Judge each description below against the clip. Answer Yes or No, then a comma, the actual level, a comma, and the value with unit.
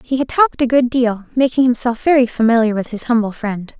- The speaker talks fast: Yes, fast, 220 wpm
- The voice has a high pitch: Yes, high, 240 Hz